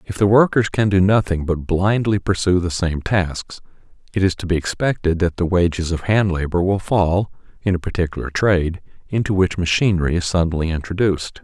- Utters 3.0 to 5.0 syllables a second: No, 5.5 syllables/s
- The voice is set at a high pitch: No, very low, 90 Hz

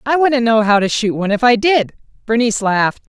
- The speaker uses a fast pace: Yes, fast, 225 wpm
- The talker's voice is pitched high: Yes, high, 230 Hz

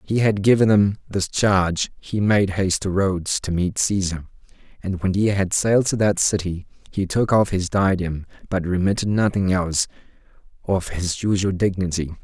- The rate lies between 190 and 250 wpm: No, average, 175 wpm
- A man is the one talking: Yes, male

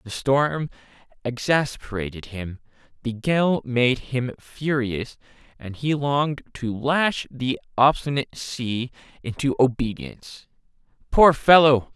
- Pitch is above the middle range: No, low, 130 Hz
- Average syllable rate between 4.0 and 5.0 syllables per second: No, 3.8 syllables/s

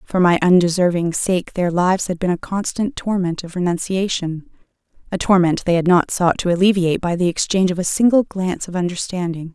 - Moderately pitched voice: Yes, medium, 180 Hz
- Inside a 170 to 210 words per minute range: Yes, average, 180 wpm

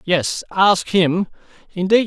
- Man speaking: Yes, male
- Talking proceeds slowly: Yes, slow, 115 wpm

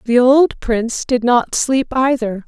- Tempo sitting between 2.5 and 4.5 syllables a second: Yes, 3.9 syllables/s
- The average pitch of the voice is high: Yes, high, 245 Hz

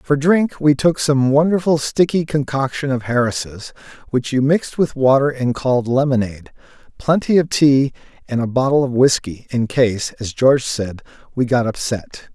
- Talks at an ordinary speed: Yes, average, 165 wpm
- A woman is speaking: No, male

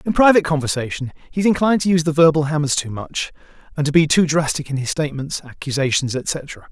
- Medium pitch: Yes, medium, 150 Hz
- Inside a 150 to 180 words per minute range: No, fast, 205 wpm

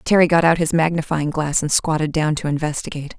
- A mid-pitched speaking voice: Yes, medium, 155 Hz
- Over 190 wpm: Yes, fast, 205 wpm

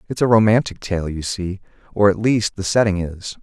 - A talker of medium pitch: No, low, 100 Hz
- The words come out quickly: Yes, fast, 210 wpm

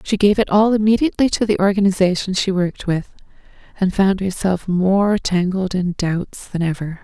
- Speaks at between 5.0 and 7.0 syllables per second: Yes, 5.1 syllables/s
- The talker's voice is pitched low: No, high, 190 Hz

